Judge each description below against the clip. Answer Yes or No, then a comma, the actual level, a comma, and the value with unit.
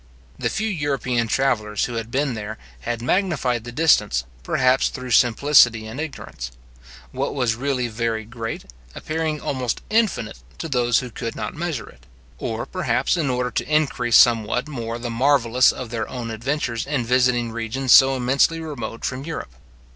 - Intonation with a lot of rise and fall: No, average, 3.4 semitones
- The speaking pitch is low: Yes, low, 125 Hz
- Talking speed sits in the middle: Yes, average, 160 wpm